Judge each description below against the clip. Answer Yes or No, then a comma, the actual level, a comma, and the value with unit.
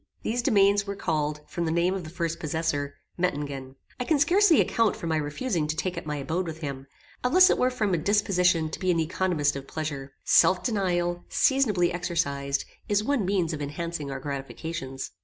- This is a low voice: No, medium, 170 Hz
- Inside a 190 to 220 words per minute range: Yes, average, 195 wpm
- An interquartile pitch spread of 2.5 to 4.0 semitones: No, average, 5.0 semitones